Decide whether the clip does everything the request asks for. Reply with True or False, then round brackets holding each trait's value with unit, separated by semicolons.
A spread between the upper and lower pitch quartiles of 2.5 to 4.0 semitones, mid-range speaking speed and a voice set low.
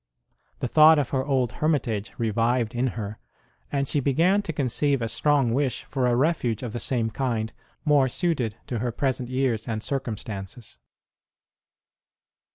True (3.7 semitones; 160 wpm; 125 Hz)